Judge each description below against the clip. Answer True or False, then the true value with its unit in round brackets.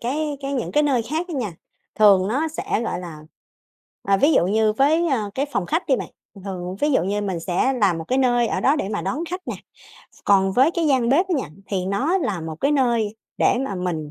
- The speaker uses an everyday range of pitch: False (6.6 semitones)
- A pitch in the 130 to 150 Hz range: False (235 Hz)